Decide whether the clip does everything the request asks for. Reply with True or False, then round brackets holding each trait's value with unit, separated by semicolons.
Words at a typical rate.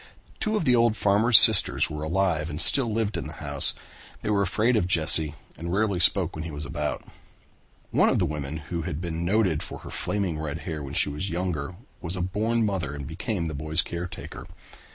False (210 wpm)